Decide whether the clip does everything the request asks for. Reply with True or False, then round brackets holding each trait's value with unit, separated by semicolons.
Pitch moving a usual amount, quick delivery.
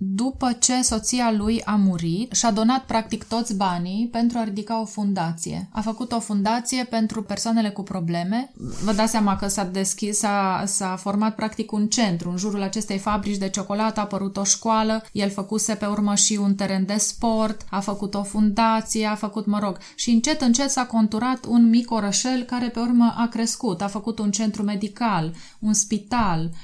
False (2.3 semitones; 185 wpm)